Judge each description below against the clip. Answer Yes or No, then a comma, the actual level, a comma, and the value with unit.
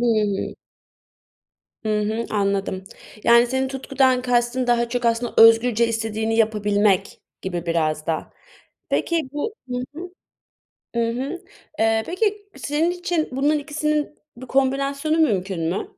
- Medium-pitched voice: No, high, 240 Hz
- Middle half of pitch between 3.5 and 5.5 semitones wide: Yes, average, 4.6 semitones